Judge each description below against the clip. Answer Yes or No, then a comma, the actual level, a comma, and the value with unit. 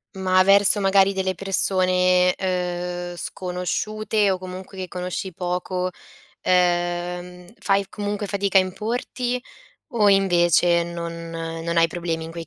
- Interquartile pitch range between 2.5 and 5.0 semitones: No, narrow, 1.8 semitones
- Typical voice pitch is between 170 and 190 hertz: Yes, medium, 185 Hz